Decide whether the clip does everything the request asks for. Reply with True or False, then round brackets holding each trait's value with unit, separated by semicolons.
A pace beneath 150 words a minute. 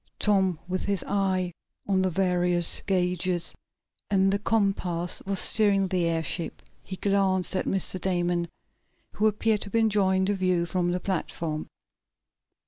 True (140 wpm)